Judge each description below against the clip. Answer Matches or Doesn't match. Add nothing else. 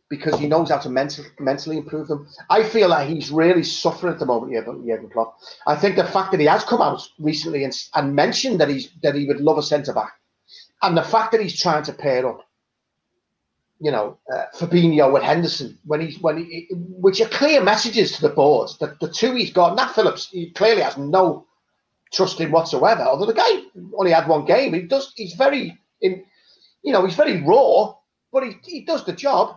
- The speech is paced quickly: Matches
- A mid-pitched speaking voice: Matches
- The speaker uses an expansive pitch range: Matches